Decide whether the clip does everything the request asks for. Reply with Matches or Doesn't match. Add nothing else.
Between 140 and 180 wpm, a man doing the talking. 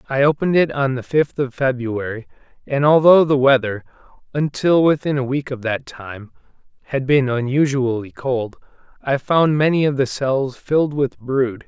Matches